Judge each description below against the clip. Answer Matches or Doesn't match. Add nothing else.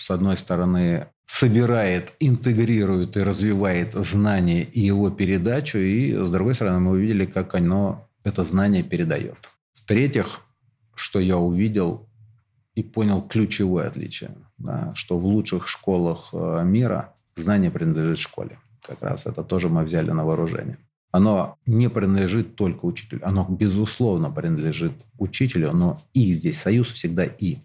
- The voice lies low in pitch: Matches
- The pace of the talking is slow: Doesn't match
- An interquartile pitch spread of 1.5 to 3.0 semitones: Doesn't match